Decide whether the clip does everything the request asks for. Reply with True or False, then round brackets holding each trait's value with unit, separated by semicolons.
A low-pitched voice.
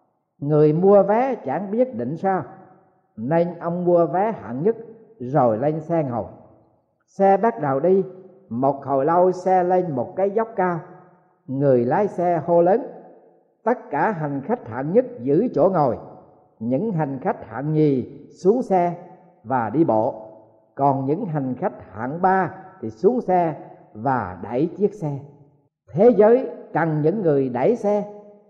False (170 Hz)